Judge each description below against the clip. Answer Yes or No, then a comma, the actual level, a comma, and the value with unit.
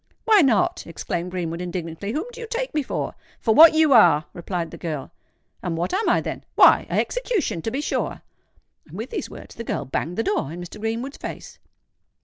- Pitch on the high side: Yes, high, 215 Hz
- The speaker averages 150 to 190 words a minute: No, average, 200 wpm